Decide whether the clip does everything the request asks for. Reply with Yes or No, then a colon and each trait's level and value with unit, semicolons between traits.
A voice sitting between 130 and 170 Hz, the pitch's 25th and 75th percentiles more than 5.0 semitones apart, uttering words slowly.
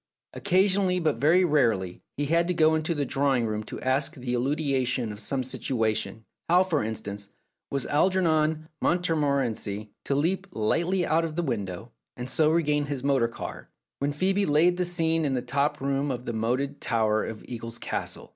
No: medium, 140 Hz; wide, 5.4 semitones; average, 185 wpm